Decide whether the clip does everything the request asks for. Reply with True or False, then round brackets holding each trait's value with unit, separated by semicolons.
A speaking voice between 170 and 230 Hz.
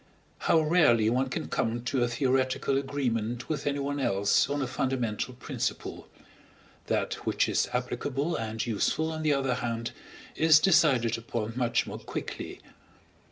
False (130 Hz)